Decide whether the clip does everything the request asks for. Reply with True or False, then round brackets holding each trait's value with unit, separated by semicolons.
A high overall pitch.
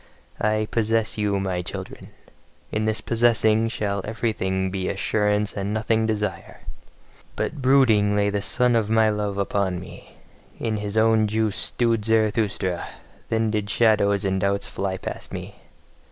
False (105 Hz)